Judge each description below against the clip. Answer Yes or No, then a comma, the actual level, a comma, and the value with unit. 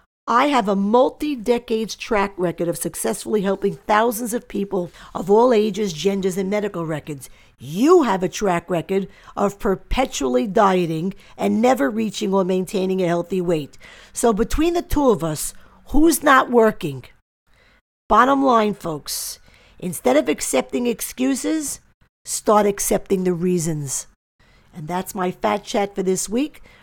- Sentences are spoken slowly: No, average, 145 wpm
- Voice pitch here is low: No, high, 200 Hz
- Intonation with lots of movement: No, average, 4.7 semitones